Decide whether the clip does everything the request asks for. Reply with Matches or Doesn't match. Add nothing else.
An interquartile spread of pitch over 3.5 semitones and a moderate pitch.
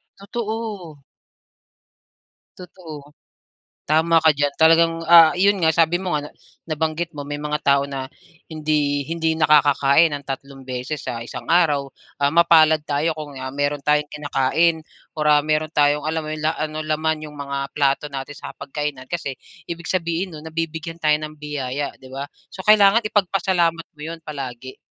Doesn't match